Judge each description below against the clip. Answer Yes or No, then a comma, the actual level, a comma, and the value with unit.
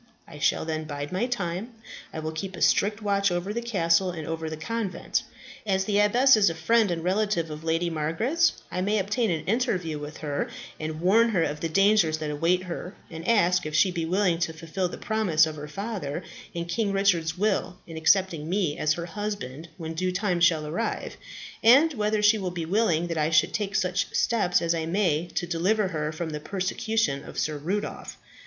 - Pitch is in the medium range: Yes, medium, 175 Hz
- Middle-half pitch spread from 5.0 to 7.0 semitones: No, average, 4.3 semitones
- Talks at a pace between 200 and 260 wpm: Yes, fast, 205 wpm